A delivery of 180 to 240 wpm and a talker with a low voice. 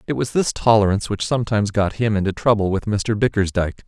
Yes: average, 200 wpm; low, 105 Hz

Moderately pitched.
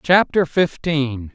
Yes: medium, 155 Hz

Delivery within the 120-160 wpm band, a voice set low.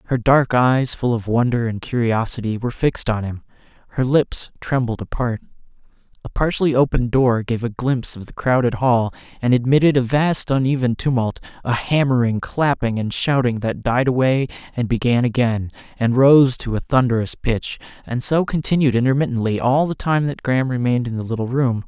No: average, 175 wpm; low, 125 Hz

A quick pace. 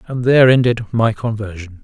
No: average, 165 wpm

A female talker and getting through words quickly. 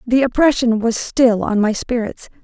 No: female; average, 170 wpm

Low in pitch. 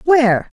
No: very high, 260 Hz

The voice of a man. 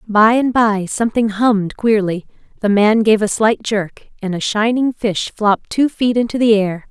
No: female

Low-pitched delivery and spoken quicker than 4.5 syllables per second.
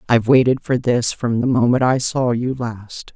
Yes: low, 120 Hz; 4.7 syllables/s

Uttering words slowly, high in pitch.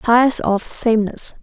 Yes: slow, 125 wpm; high, 230 Hz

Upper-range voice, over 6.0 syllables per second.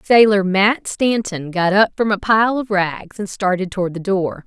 No: high, 195 Hz; 4.4 syllables/s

